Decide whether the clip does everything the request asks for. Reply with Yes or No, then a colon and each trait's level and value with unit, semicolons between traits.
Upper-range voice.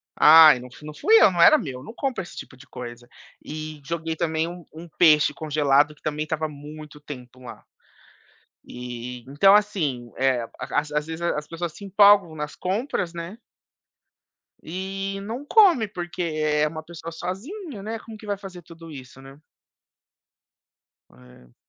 No: medium, 160 Hz